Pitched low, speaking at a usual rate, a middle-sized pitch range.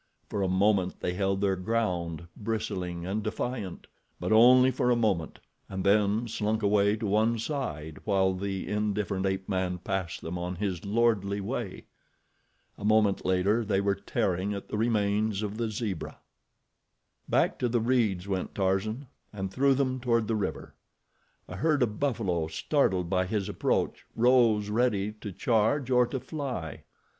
Yes: low, 105 Hz; average, 160 wpm; average, 3.3 semitones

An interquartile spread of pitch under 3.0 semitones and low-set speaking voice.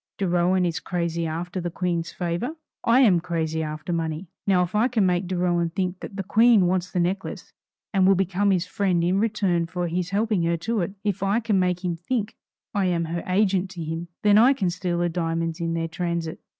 No: narrow, 2.5 semitones; medium, 180 Hz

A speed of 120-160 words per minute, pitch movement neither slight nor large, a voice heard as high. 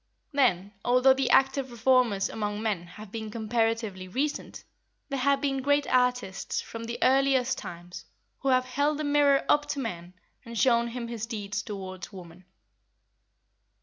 Yes: average, 150 wpm; average, 4.5 semitones; high, 235 Hz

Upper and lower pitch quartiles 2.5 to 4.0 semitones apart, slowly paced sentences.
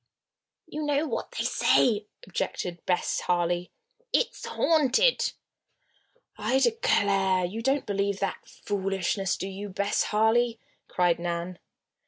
No: average, 5.0 semitones; slow, 115 wpm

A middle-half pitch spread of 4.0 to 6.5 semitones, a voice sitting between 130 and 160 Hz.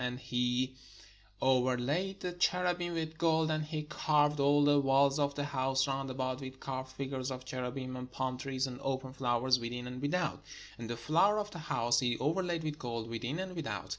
No: average, 3.3 semitones; low, 135 Hz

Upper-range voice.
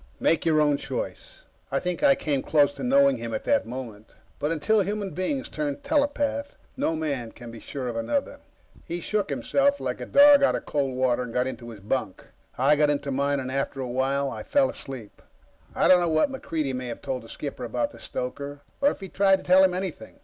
No: medium, 150 Hz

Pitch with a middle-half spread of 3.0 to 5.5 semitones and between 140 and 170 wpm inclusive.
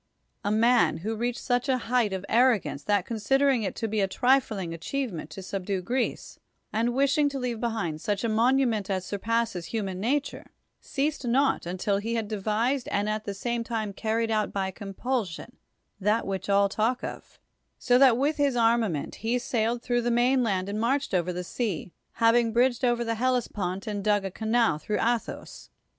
No: average, 3.5 semitones; average, 195 wpm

